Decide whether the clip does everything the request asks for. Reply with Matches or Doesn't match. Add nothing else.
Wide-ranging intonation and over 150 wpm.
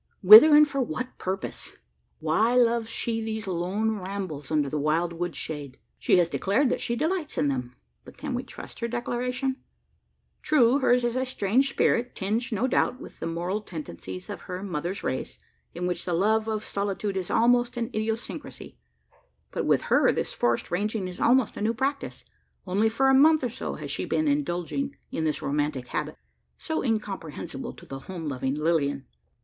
Matches